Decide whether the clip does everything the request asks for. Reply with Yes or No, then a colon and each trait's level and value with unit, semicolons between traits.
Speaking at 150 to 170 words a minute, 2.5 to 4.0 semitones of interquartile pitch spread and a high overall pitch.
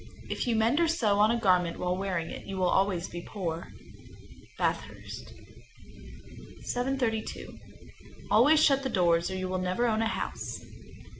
No: average, 160 wpm; average, 4.6 semitones; high, 200 Hz